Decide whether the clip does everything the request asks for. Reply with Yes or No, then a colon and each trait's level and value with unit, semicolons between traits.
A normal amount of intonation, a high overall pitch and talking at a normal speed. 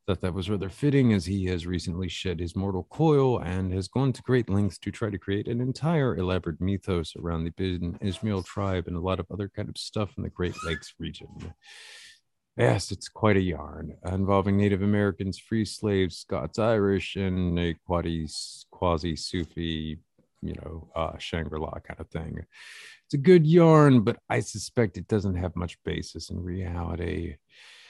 No: average, 3.4 semitones; very low, 95 Hz; average, 175 wpm